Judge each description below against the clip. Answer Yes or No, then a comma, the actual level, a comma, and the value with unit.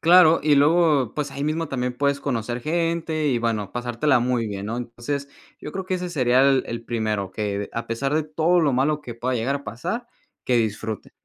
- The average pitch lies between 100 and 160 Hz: Yes, low, 135 Hz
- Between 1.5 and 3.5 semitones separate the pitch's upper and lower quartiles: No, average, 4.7 semitones